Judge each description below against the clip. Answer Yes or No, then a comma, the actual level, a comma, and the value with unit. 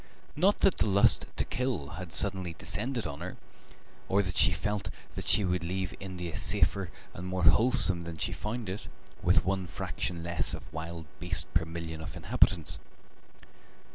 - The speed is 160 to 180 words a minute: Yes, average, 170 wpm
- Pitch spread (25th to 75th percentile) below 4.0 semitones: Yes, average, 2.9 semitones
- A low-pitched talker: Yes, very low, 90 Hz